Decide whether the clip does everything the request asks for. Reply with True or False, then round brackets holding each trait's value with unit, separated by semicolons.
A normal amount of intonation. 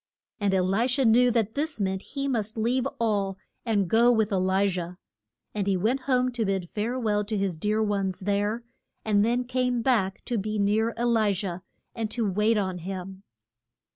True (3.4 semitones)